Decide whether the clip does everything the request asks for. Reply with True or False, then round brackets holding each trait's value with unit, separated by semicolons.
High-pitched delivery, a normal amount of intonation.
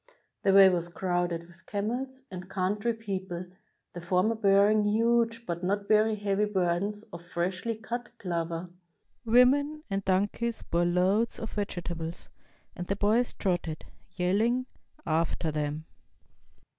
True (195 Hz; 4.1 semitones)